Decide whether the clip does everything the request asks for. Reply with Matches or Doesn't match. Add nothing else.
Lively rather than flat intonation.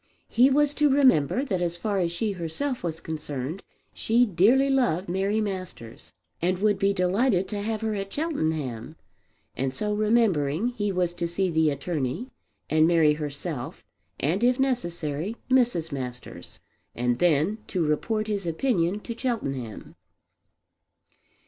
Matches